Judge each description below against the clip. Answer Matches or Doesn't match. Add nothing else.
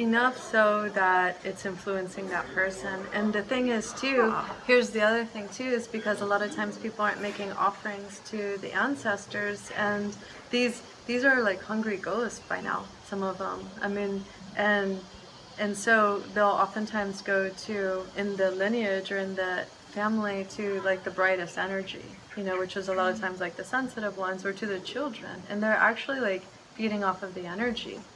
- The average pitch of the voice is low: Doesn't match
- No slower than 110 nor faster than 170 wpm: Doesn't match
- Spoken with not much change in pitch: Matches